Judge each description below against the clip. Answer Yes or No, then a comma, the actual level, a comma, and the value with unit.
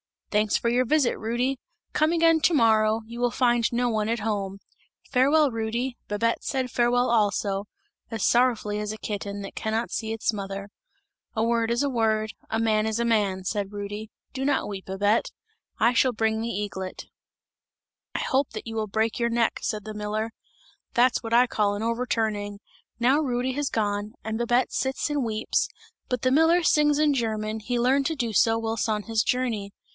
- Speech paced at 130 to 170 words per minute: No, average, 190 wpm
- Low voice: No, high, 225 Hz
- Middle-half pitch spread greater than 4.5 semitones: No, average, 2.7 semitones